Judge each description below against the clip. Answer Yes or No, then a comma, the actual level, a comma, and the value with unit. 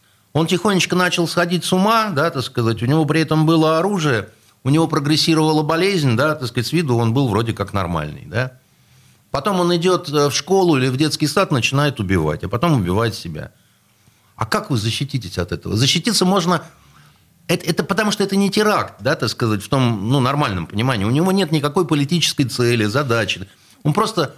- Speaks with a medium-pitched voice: Yes, medium, 145 Hz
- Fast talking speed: Yes, fast, 190 wpm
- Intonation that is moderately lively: No, wide, 6.9 semitones